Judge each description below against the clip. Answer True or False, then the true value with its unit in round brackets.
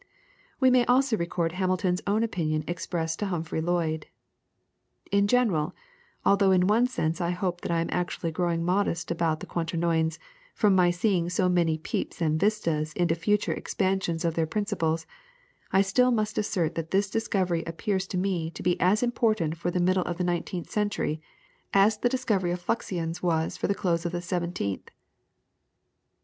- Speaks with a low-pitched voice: False (180 Hz)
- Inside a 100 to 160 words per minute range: False (170 wpm)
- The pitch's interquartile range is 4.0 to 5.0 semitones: False (3.3 semitones)